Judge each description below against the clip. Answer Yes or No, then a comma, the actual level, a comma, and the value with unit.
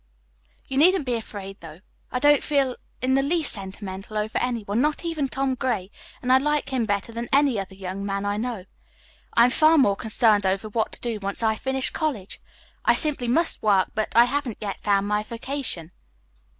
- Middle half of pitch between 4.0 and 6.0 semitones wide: Yes, average, 5.1 semitones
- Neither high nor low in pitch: No, high, 230 Hz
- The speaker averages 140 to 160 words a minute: No, average, 200 wpm